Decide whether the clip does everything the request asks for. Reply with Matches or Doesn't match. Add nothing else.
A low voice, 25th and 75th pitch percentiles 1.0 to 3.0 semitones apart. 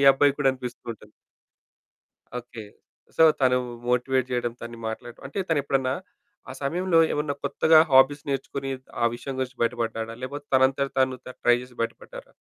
Matches